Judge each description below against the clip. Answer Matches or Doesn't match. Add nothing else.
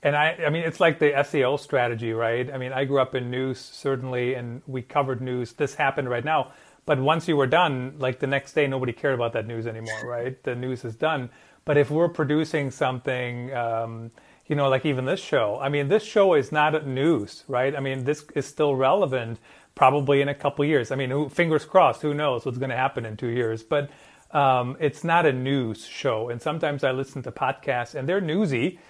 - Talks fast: Matches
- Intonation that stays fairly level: Doesn't match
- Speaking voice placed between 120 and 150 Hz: Matches